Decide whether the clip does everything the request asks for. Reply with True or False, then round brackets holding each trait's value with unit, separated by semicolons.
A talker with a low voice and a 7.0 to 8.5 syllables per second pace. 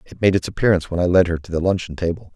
True (90 Hz; 7.6 syllables/s)